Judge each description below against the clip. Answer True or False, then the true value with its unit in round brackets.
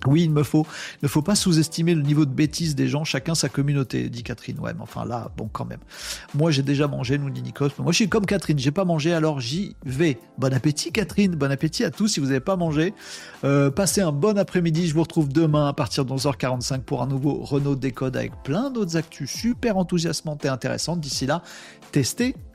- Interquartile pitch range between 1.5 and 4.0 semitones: True (3.5 semitones)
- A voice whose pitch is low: False (155 Hz)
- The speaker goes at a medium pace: False (225 wpm)